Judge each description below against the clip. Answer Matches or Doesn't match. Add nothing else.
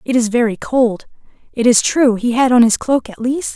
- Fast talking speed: Matches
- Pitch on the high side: Matches